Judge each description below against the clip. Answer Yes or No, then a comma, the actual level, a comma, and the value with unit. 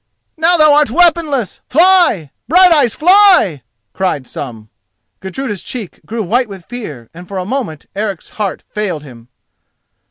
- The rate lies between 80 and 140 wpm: Yes, slow, 135 wpm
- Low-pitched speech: No, high, 215 Hz